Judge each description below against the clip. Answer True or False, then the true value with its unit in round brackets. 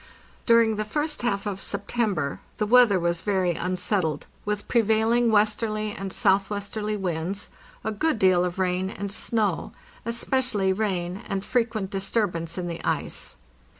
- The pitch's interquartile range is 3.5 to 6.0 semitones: False (2.9 semitones)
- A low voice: False (205 Hz)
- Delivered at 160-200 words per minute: False (145 wpm)